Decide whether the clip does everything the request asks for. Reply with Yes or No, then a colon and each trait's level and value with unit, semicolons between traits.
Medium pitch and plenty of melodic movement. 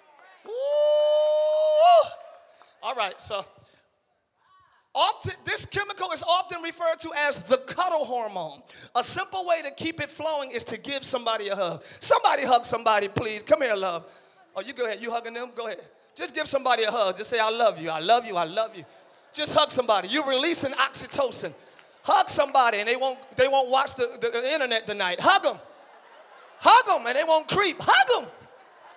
No: very high, 290 Hz; wide, 6.1 semitones